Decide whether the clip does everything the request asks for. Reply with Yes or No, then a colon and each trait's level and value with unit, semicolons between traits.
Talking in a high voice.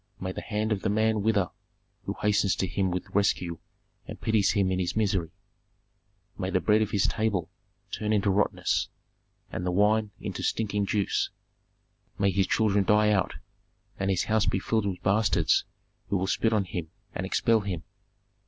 No: low, 100 Hz